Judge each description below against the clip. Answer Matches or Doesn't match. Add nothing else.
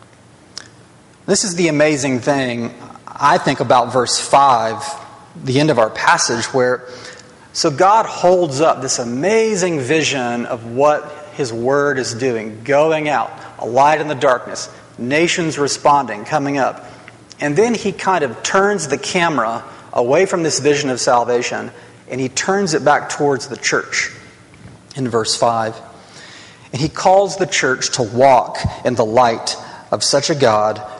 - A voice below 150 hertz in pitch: Matches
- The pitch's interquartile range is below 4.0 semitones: Doesn't match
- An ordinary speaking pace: Matches